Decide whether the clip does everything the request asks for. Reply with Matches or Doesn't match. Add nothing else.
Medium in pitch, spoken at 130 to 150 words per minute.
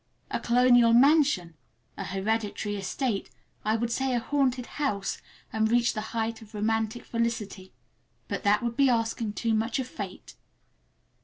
Doesn't match